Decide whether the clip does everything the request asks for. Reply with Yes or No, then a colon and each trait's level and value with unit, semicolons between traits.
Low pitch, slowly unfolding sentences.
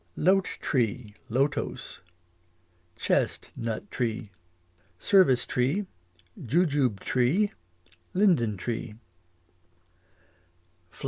Yes: low, 125 Hz; slow, 65 wpm